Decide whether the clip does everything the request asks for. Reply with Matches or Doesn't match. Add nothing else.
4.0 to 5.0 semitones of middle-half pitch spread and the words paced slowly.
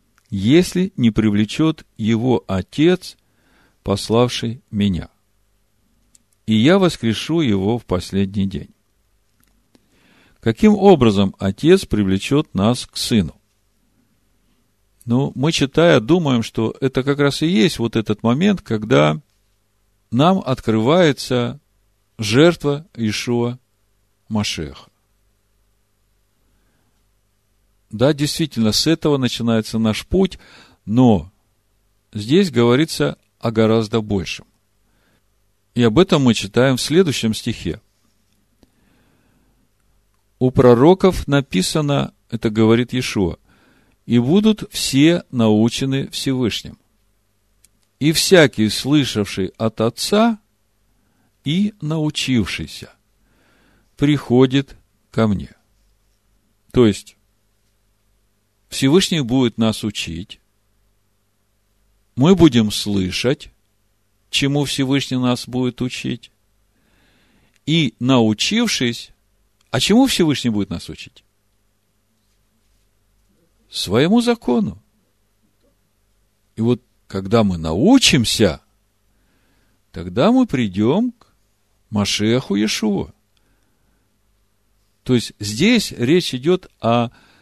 Matches